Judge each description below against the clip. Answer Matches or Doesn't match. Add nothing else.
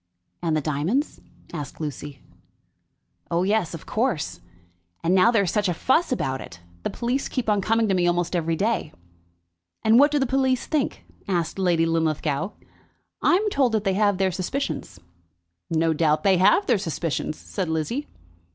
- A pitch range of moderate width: Doesn't match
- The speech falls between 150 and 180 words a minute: Matches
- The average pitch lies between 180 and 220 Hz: Matches